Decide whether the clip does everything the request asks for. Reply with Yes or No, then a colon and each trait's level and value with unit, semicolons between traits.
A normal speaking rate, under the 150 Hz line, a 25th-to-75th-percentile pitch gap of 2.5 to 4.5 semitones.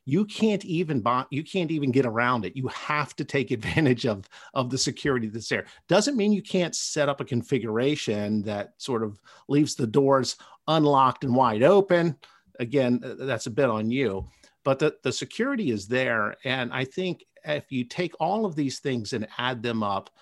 Yes: average, 195 wpm; low, 135 Hz; average, 3.9 semitones